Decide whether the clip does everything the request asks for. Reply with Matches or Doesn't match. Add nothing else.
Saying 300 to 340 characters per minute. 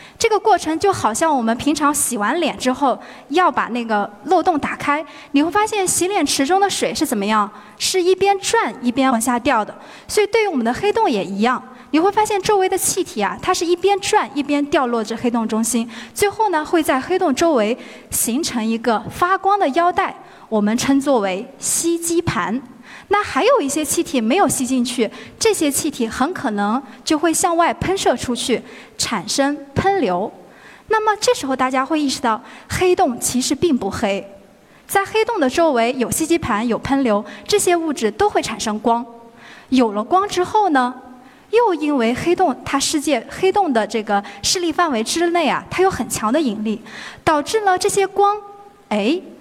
Doesn't match